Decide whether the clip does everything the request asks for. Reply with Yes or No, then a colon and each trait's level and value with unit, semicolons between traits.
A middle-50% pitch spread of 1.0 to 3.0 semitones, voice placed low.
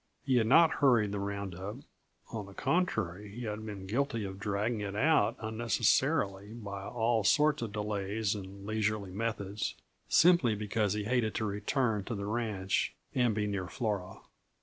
Yes: narrow, 2.6 semitones; low, 105 Hz